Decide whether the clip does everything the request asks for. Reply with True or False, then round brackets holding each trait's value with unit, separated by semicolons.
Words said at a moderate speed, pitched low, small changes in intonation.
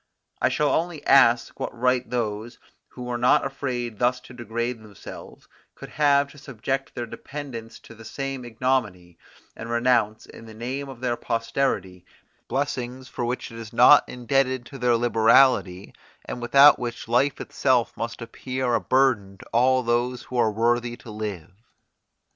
True (160 wpm; 120 Hz; 2.3 semitones)